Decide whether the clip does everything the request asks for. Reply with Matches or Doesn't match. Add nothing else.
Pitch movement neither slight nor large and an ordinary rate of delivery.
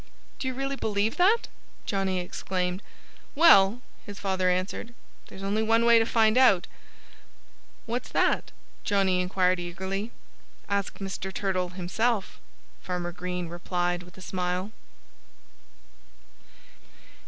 Doesn't match